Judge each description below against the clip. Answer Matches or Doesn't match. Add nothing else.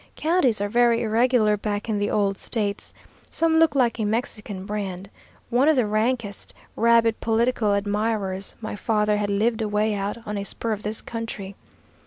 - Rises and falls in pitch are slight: Matches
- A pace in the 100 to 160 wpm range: Doesn't match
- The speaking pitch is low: Doesn't match